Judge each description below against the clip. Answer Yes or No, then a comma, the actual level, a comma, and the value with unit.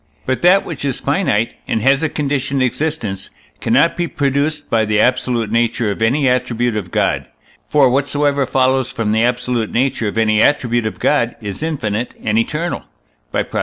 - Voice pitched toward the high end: No, low, 125 Hz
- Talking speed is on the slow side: No, average, 175 wpm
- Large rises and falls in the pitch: No, average, 4.1 semitones